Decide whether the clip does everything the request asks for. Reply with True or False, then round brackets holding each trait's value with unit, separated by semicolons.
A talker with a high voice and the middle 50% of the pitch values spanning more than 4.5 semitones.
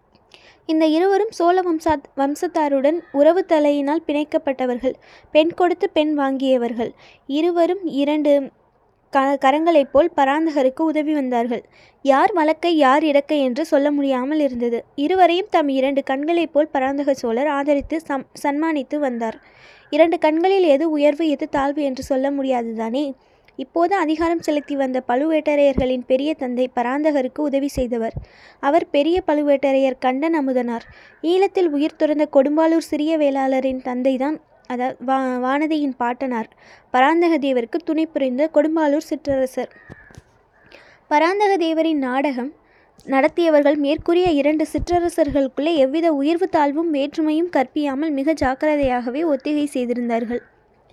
False (290 Hz; 3.0 semitones)